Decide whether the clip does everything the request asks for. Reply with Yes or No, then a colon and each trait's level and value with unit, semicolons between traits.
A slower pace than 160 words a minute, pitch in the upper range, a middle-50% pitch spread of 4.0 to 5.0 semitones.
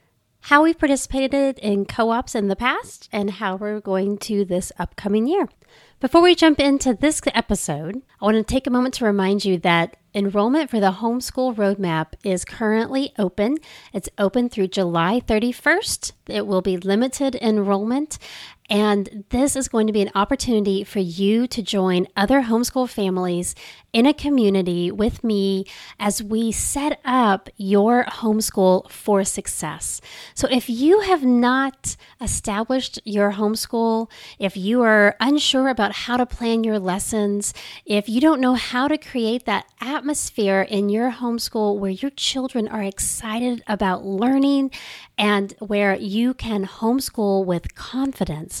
Yes: average, 150 wpm; high, 220 Hz; average, 4.3 semitones